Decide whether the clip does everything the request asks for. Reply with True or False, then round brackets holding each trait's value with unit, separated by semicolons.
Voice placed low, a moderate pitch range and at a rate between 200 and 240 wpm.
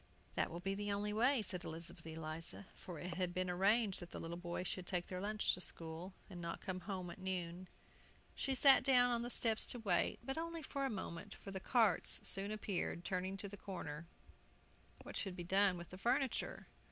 False (190 Hz; 3.4 semitones; 205 wpm)